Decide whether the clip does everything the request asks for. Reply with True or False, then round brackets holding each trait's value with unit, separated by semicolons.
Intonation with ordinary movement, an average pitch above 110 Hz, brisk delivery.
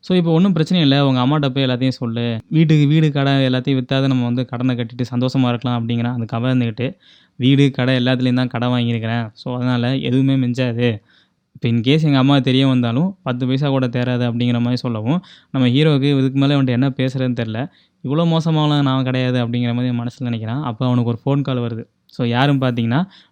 False (2.3 semitones; 130 Hz; 185 wpm)